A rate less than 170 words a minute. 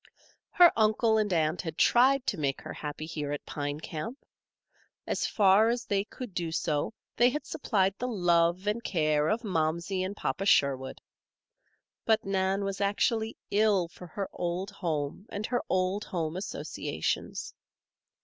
Yes: average, 155 wpm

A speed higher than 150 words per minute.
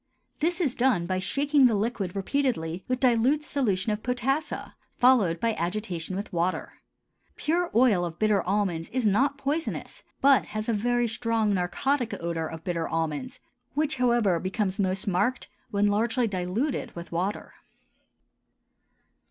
No: average, 145 wpm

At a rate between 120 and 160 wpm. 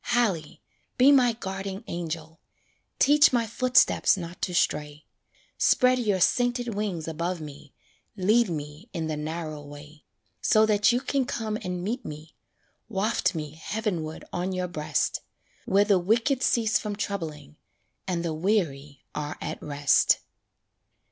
Yes: average, 140 wpm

